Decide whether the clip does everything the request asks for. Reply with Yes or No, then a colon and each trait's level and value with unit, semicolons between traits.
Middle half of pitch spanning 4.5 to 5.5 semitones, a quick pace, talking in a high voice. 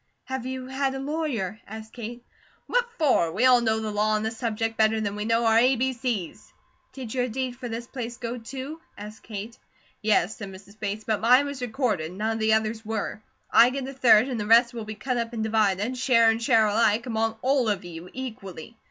No: average, 2.8 semitones; fast, 220 wpm; high, 225 Hz